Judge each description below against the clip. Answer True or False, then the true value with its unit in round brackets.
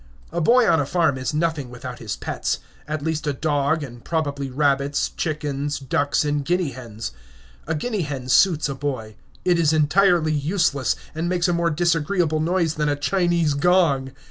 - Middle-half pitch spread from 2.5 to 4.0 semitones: True (3.4 semitones)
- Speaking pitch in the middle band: True (150 Hz)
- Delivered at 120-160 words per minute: False (175 wpm)